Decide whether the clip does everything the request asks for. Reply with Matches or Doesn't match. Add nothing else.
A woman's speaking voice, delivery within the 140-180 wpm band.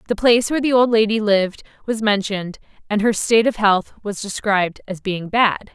Doesn't match